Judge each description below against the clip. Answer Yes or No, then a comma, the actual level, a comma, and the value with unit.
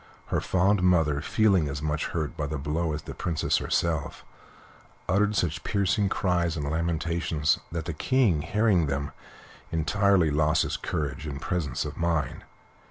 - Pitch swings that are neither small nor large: Yes, average, 3.3 semitones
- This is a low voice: Yes, very low, 80 Hz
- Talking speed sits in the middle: Yes, average, 155 wpm